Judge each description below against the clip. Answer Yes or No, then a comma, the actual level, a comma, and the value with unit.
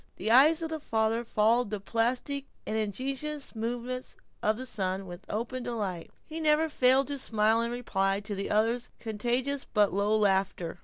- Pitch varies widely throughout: No, average, 3.7 semitones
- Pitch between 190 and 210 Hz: No, high, 230 Hz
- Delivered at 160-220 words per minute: Yes, average, 175 wpm